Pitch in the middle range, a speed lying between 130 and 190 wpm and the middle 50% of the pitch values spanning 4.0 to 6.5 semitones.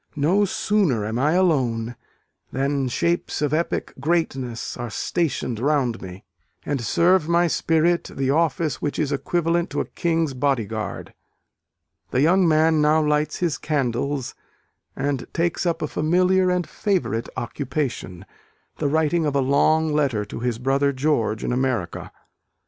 Yes: medium, 145 Hz; average, 145 wpm; average, 4.6 semitones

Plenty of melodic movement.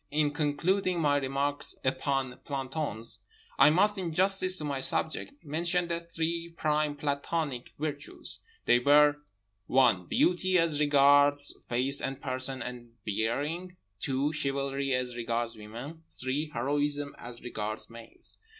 No: average, 3.5 semitones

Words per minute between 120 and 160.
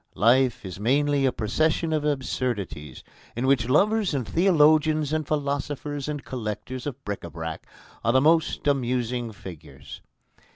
Yes: average, 140 wpm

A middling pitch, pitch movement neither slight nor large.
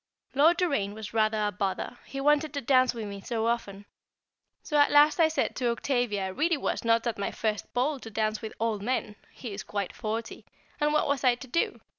No: high, 235 Hz; average, 4.9 semitones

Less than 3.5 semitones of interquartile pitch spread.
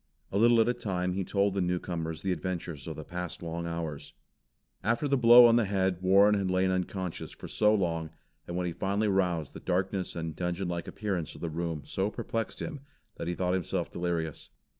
Yes: average, 2.8 semitones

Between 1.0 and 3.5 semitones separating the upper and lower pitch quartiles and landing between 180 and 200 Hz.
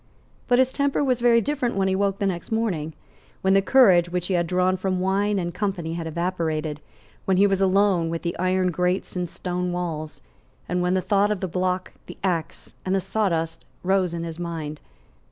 Yes: narrow, 2.4 semitones; medium, 185 Hz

